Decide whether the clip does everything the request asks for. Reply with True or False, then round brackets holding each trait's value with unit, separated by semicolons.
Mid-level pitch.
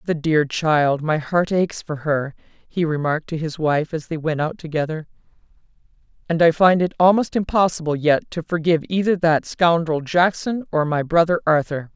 True (160 Hz)